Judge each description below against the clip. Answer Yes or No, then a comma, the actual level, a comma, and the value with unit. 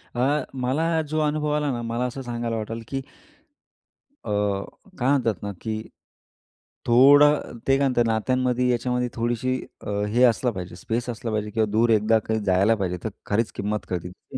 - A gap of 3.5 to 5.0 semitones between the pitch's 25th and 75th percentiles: No, average, 2.7 semitones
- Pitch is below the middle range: Yes, low, 120 Hz